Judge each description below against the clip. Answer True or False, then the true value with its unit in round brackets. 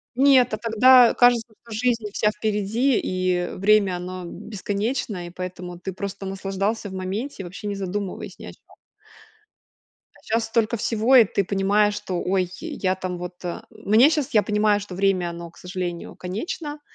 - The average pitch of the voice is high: True (200 Hz)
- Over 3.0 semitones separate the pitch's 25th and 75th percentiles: True (3.5 semitones)